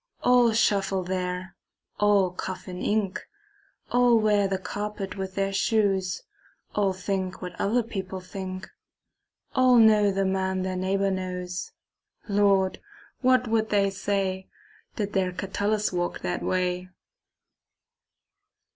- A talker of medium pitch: No, high, 195 Hz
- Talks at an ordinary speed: No, slow, 120 wpm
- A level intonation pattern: Yes, narrow, 1.9 semitones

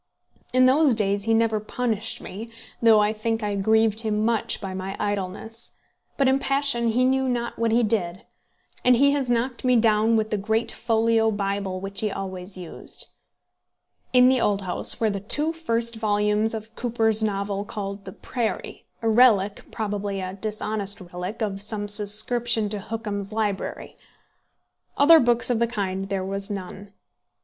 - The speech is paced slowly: No, average, 165 wpm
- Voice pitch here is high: Yes, high, 215 Hz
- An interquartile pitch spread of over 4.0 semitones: No, narrow, 2.6 semitones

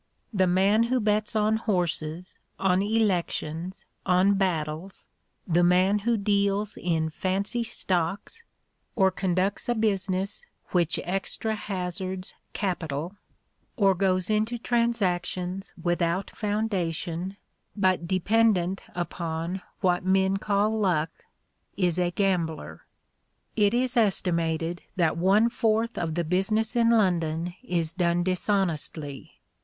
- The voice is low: No, high, 190 Hz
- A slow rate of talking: Yes, slow, 110 wpm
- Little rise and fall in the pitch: No, average, 3.2 semitones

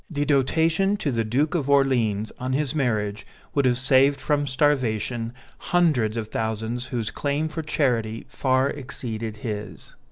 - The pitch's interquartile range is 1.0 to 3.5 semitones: No, average, 4.4 semitones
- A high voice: No, low, 130 Hz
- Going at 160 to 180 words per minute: No, average, 150 wpm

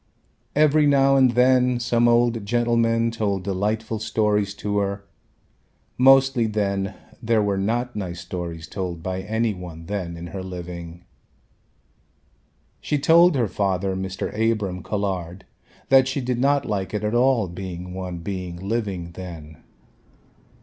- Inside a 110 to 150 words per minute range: Yes, slow, 135 wpm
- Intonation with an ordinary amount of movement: Yes, average, 4.4 semitones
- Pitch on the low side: Yes, low, 105 Hz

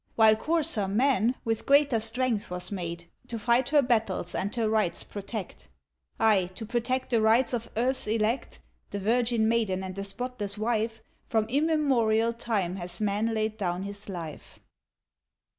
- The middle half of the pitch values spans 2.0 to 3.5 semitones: Yes, average, 3.1 semitones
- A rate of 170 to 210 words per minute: No, average, 155 wpm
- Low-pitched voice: No, high, 220 Hz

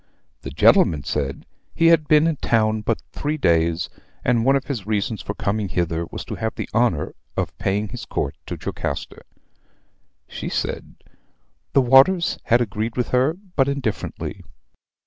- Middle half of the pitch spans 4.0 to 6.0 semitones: Yes, wide, 5.5 semitones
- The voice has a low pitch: Yes, low, 115 Hz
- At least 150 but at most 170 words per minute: Yes, average, 160 wpm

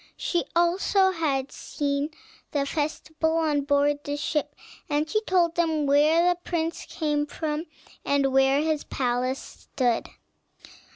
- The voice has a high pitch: Yes, very high, 300 Hz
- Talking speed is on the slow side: Yes, slow, 125 wpm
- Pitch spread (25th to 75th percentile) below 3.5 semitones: Yes, narrow, 2.5 semitones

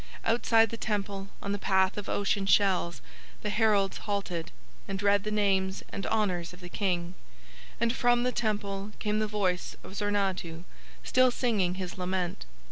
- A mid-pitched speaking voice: No, high, 200 Hz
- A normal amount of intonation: No, narrow, 2.2 semitones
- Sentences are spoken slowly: No, average, 160 wpm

